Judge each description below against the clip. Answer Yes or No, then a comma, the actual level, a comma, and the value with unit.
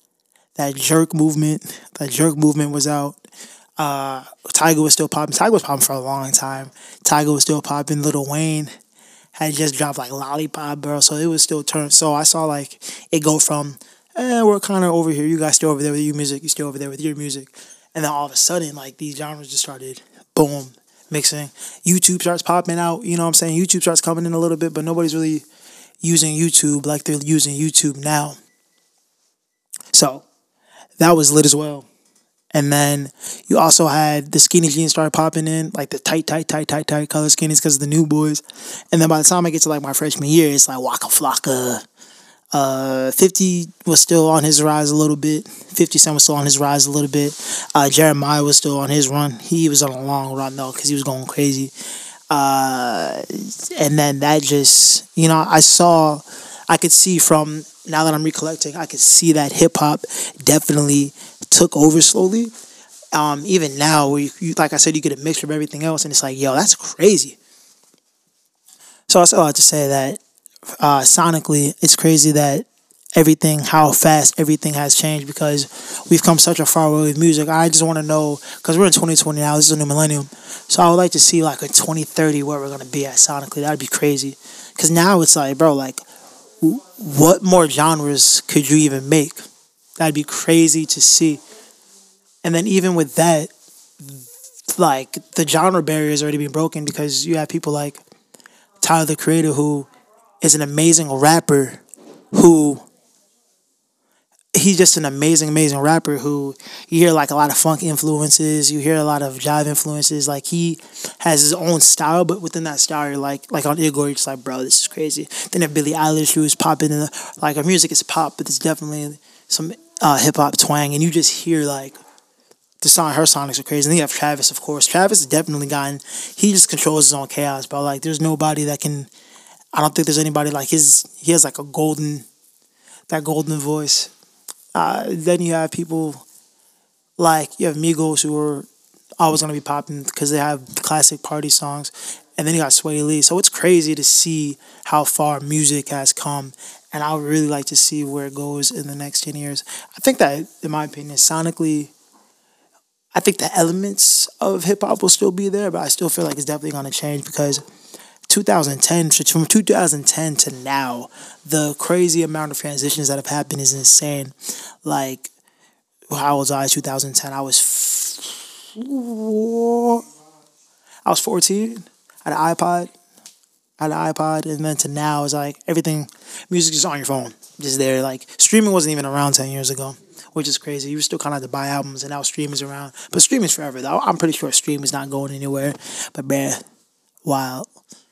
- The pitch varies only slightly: Yes, narrow, 2.1 semitones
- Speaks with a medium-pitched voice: Yes, medium, 150 Hz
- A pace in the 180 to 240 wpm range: Yes, average, 200 wpm